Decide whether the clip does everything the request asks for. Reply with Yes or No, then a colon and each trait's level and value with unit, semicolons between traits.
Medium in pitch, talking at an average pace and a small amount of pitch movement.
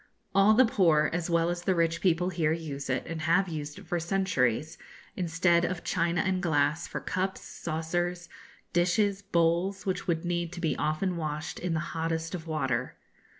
Yes: medium, 170 Hz; average, 180 wpm; narrow, 2.2 semitones